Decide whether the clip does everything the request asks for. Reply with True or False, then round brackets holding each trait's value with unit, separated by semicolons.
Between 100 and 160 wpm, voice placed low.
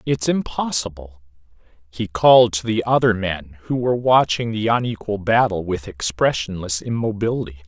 True (135 wpm; 105 Hz)